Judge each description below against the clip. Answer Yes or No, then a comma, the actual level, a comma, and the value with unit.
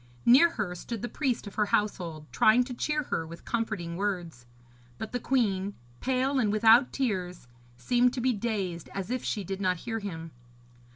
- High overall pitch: Yes, high, 210 Hz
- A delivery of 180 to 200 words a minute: Yes, average, 185 wpm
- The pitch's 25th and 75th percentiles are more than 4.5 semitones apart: Yes, average, 5.1 semitones